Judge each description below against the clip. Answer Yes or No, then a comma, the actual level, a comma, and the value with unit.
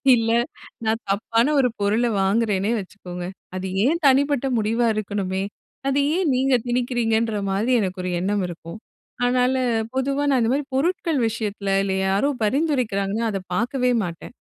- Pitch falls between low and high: No, high, 225 Hz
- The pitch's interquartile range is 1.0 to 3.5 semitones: No, average, 4.7 semitones